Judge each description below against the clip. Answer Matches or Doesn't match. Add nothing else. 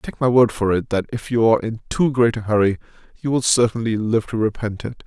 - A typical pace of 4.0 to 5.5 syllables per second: Doesn't match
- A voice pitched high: Doesn't match